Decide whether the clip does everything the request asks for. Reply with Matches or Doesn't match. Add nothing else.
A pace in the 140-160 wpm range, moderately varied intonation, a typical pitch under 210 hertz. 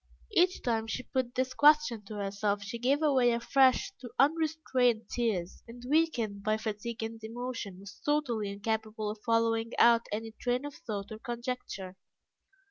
Doesn't match